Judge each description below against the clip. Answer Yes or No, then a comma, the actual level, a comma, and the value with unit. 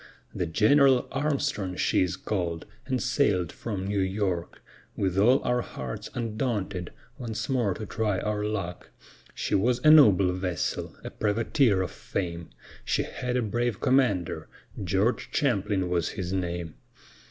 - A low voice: Yes, low, 105 Hz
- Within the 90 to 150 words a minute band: Yes, average, 140 wpm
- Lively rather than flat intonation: No, average, 4.9 semitones